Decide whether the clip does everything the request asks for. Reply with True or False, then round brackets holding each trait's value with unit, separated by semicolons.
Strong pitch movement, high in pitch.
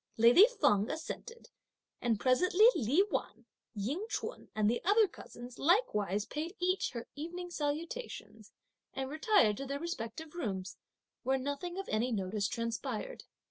True (7.9 semitones; 280 Hz)